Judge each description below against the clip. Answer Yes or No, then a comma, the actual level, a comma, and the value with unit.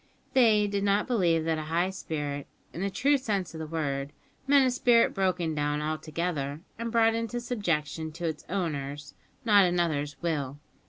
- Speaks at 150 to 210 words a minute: Yes, average, 170 wpm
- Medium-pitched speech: Yes, medium, 170 Hz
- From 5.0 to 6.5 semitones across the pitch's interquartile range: Yes, wide, 5.6 semitones